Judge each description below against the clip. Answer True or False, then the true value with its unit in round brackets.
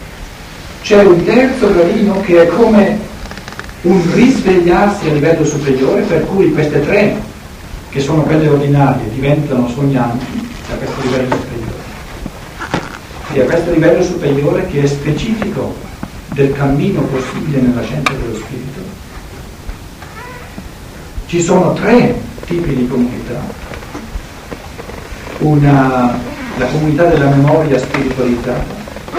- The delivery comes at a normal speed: False (110 wpm)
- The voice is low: False (145 Hz)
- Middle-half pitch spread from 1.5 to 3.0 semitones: False (5.5 semitones)